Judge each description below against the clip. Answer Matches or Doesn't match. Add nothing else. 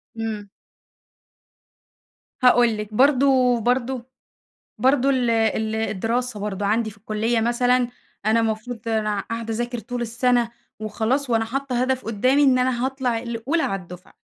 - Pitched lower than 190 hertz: Doesn't match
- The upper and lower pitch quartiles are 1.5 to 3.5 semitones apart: Matches